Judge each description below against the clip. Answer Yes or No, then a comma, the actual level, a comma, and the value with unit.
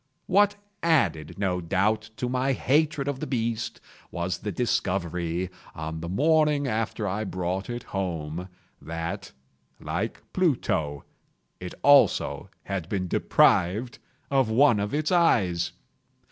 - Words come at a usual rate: No, slow, 125 wpm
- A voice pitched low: Yes, low, 100 Hz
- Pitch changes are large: Yes, wide, 7.1 semitones